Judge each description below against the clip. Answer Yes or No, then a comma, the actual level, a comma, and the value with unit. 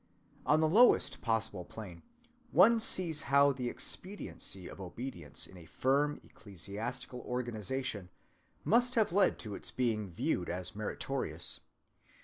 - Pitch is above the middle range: No, low, 125 Hz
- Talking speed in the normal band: No, slow, 130 wpm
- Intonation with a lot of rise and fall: Yes, wide, 7.0 semitones